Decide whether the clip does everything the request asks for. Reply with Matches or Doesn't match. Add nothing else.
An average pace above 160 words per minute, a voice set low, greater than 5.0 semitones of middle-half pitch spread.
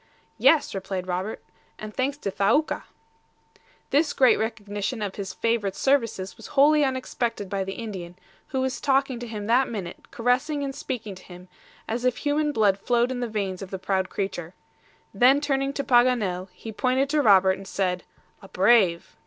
Doesn't match